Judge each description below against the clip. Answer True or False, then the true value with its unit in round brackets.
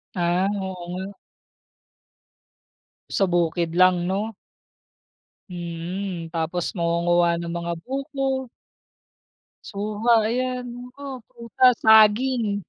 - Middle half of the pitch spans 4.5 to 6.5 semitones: True (5.1 semitones)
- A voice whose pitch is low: False (190 Hz)